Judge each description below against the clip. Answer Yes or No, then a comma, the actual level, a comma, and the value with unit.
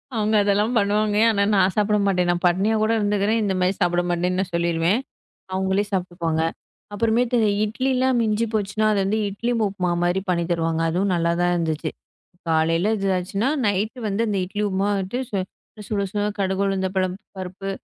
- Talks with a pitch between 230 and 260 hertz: No, high, 195 Hz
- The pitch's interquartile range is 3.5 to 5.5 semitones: No, average, 2.8 semitones